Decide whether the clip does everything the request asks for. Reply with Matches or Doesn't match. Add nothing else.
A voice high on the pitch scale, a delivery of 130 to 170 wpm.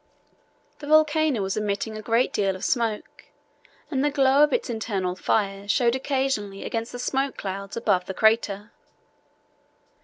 Matches